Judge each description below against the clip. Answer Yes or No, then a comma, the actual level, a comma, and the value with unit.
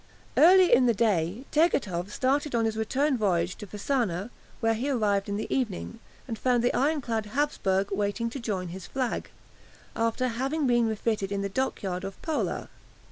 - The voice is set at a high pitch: Yes, high, 225 Hz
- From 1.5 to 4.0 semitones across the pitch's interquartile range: No, average, 4.6 semitones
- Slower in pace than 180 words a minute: Yes, average, 170 wpm